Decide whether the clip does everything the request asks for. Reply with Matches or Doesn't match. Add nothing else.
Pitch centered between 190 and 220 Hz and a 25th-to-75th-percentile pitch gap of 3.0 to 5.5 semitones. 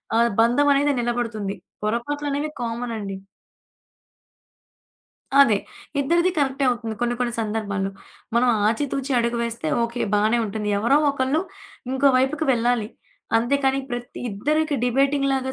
Doesn't match